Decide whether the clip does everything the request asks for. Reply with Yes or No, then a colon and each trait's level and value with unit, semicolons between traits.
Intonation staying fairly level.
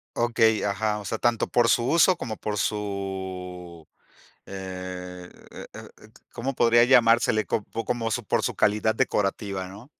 No: average, 3.7 semitones